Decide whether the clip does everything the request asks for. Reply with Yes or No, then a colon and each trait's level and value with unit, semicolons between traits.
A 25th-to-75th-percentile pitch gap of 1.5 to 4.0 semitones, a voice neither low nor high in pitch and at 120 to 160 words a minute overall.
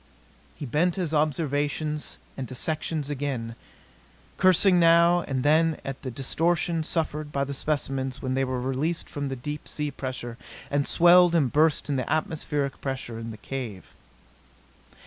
Yes: average, 3.3 semitones; medium, 145 Hz; average, 155 wpm